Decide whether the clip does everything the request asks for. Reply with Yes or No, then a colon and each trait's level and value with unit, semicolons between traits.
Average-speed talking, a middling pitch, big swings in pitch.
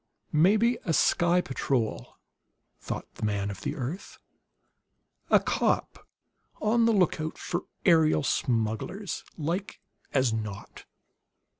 No: slow, 110 wpm; medium, 155 Hz; wide, 8.2 semitones